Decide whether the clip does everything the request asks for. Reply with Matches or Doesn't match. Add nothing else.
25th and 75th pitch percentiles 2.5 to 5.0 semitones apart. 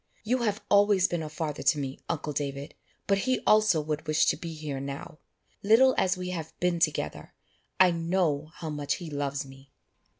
Matches